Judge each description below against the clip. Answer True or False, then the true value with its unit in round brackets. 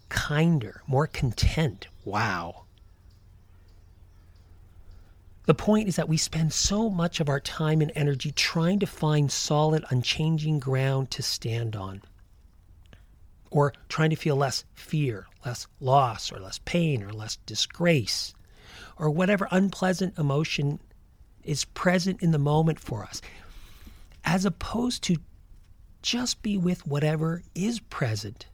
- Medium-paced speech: False (125 wpm)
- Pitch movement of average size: False (9.0 semitones)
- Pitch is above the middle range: False (135 Hz)